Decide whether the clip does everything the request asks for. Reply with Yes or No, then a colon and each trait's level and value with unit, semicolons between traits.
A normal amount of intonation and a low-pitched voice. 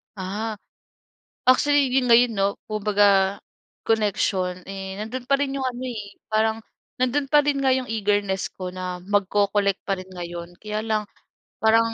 No: average, 4.0 semitones; high, 210 Hz